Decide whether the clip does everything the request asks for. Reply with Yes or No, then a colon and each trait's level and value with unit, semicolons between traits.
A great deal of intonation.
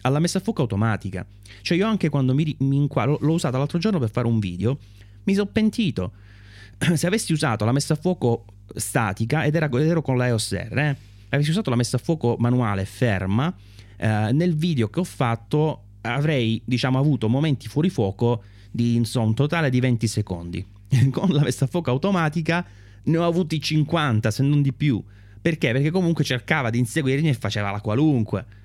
Yes: wide, 6.4 semitones